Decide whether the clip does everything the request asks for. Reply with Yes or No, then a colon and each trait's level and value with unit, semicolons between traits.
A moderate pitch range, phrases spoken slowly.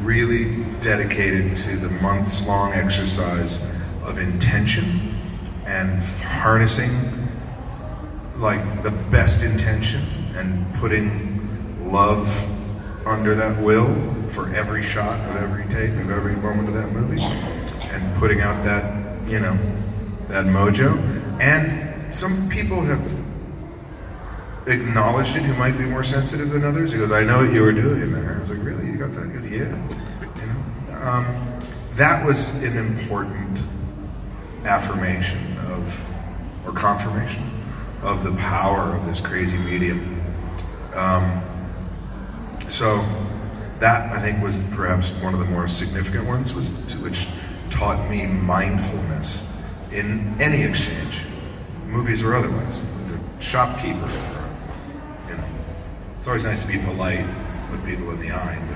Yes: average, 3.3 semitones; slow, 130 wpm